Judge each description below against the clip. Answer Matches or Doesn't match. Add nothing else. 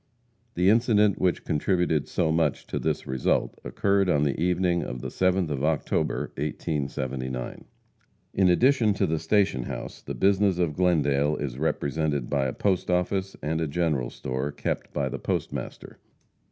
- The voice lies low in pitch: Matches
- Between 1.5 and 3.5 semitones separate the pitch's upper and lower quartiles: Doesn't match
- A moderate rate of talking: Matches